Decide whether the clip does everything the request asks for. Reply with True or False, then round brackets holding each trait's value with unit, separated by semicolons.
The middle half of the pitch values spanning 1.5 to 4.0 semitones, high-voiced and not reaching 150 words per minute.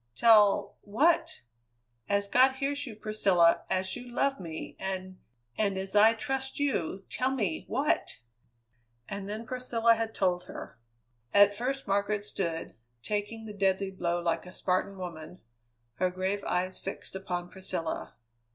True (3.7 semitones; 200 Hz; 140 wpm)